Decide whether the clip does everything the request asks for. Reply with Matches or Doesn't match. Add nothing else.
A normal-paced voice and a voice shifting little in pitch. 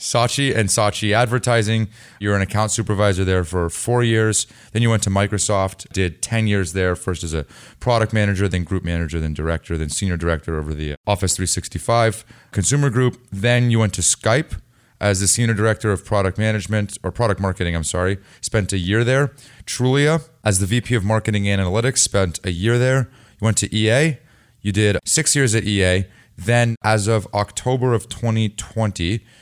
Doesn't match